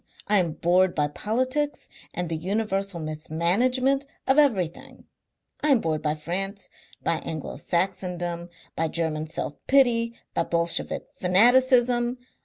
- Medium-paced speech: No, slow, 125 wpm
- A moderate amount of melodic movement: No, wide, 6.5 semitones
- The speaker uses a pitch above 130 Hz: Yes, medium, 185 Hz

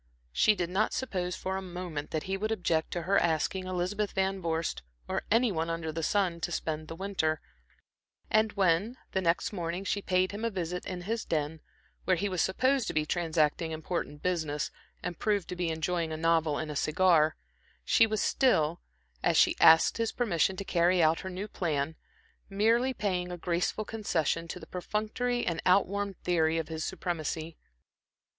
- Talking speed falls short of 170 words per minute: No, average, 185 wpm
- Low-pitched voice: No, medium, 180 Hz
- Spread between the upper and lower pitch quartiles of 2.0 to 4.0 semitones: Yes, average, 3.5 semitones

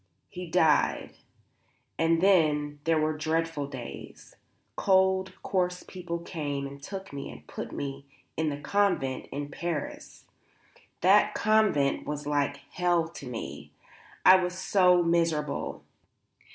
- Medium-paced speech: No, slow, 125 wpm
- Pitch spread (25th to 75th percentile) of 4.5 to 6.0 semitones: No, average, 4.0 semitones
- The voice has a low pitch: No, medium, 165 Hz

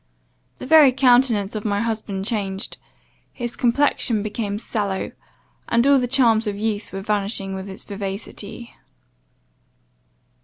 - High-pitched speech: Yes, high, 215 Hz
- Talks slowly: Yes, slow, 125 wpm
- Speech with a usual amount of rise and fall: Yes, average, 3.1 semitones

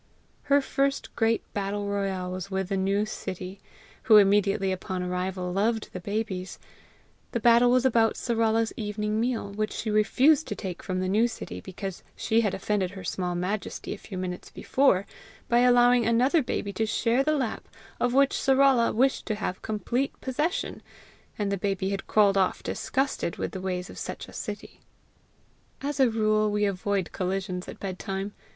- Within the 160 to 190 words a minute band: Yes, average, 170 wpm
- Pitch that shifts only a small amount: No, average, 3.7 semitones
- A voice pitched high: Yes, high, 210 Hz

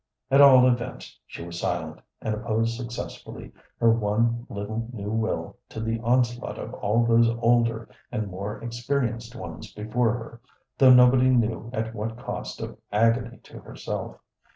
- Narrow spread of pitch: Yes, narrow, 1.8 semitones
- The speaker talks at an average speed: Yes, average, 155 wpm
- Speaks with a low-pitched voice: Yes, low, 115 Hz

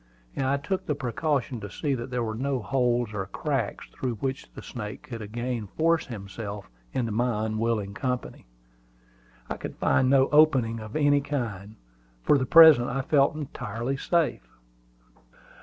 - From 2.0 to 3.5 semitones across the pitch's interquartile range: No, average, 4.2 semitones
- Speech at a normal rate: Yes, average, 155 wpm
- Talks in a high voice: No, low, 125 Hz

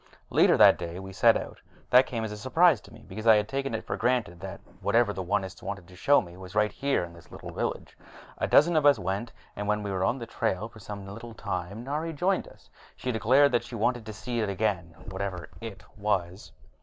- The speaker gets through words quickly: Yes, fast, 235 wpm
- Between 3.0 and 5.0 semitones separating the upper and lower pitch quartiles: Yes, average, 4.2 semitones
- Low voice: Yes, low, 105 Hz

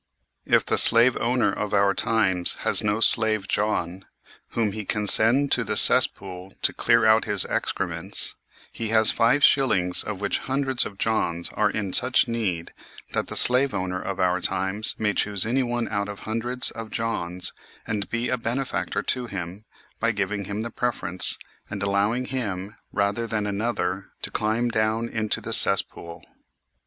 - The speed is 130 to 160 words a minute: No, average, 170 wpm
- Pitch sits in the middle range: No, low, 105 Hz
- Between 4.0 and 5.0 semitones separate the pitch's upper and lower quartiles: No, average, 3.1 semitones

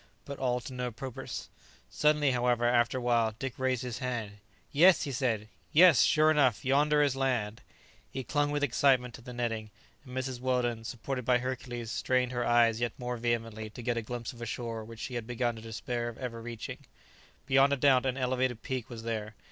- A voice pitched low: Yes, low, 125 Hz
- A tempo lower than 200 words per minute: No, fast, 205 wpm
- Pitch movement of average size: No, narrow, 2.0 semitones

